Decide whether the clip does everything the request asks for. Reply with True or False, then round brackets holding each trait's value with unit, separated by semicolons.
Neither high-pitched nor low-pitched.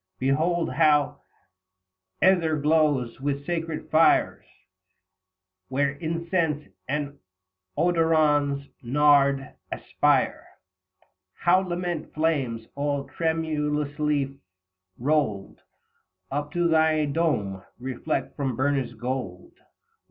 True (150 Hz)